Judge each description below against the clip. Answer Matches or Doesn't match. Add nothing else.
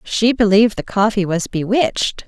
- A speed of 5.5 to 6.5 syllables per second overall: Doesn't match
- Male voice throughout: Doesn't match